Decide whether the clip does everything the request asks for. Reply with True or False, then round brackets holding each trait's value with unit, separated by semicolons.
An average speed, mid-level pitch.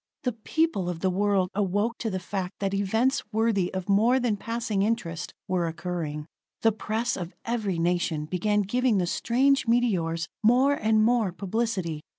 False (165 wpm; 205 Hz)